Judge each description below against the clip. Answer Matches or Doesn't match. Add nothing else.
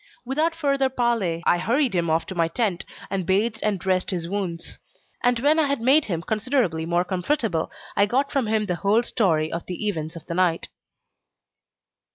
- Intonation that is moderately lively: Doesn't match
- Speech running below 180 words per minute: Doesn't match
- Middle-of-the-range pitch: Doesn't match